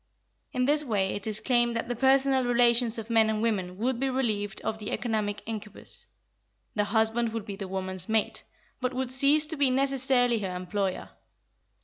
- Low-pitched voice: No, high, 230 Hz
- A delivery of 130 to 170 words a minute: No, average, 180 wpm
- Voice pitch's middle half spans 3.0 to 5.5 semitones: Yes, average, 3.7 semitones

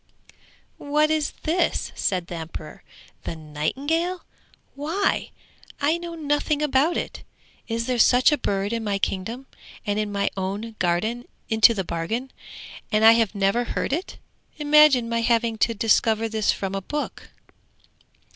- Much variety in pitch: Yes, wide, 6.5 semitones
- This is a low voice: No, high, 230 Hz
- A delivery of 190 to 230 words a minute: No, average, 150 wpm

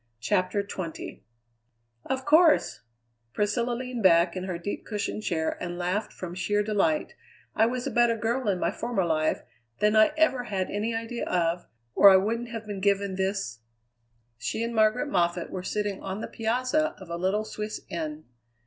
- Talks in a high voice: Yes, high, 205 Hz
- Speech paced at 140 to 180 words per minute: Yes, average, 175 wpm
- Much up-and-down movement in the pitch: No, average, 4.3 semitones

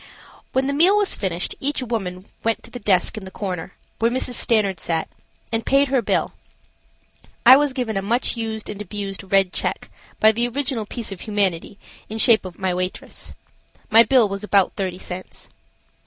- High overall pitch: Yes, high, 215 Hz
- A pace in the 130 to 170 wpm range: No, average, 185 wpm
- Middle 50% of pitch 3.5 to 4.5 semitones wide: Yes, average, 4.1 semitones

